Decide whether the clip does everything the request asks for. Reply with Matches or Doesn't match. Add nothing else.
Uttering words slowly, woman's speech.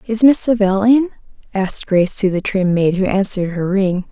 Doesn't match